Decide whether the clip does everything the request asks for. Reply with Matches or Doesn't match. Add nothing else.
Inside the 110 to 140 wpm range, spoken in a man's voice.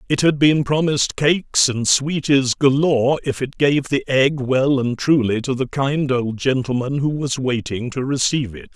Doesn't match